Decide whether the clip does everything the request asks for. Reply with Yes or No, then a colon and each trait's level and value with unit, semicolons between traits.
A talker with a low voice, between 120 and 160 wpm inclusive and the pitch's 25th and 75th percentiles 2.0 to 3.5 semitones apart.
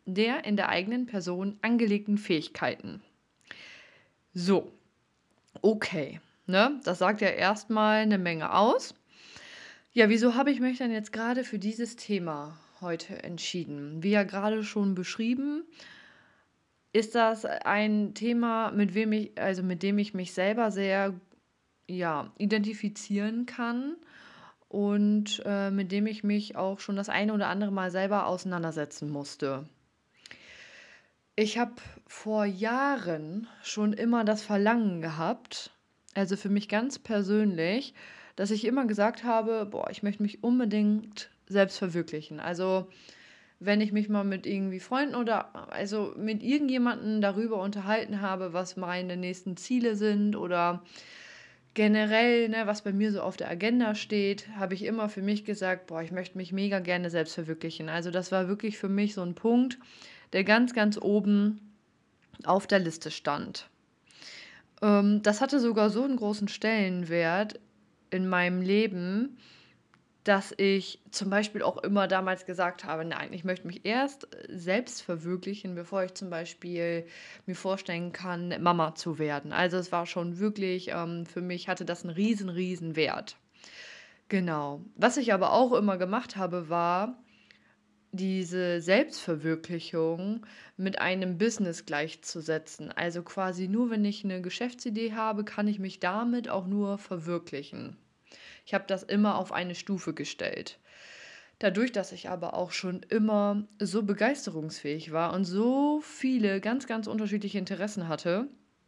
No: high, 200 Hz; average, 145 wpm; average, 3.1 semitones